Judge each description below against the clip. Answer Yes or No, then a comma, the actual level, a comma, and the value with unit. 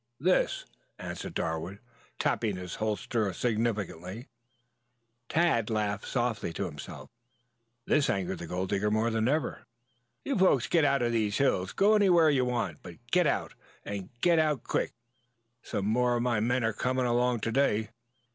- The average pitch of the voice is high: No, low, 115 Hz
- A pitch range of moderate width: Yes, average, 4.3 semitones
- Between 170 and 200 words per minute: No, average, 160 wpm